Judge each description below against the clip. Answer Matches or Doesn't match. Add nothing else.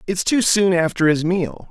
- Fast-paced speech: Matches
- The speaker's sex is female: Doesn't match